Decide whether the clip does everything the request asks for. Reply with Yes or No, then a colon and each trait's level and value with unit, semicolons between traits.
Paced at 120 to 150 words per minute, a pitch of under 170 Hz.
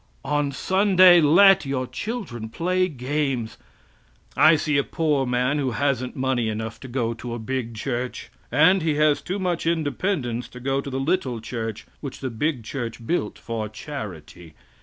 No: average, 165 wpm; low, 135 Hz